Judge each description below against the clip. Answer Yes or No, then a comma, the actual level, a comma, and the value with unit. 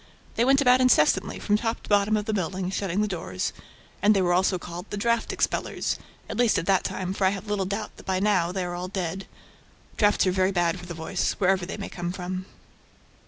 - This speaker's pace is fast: Yes, fast, 230 wpm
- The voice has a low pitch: No, high, 190 Hz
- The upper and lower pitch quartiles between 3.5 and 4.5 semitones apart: No, narrow, 2.6 semitones